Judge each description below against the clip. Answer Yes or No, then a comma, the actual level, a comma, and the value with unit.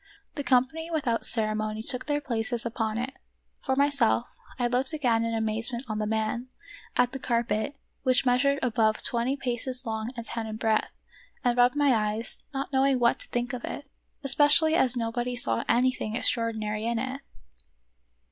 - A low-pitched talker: No, high, 240 Hz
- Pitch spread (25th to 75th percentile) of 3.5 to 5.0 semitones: No, average, 2.9 semitones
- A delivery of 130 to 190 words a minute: Yes, average, 175 wpm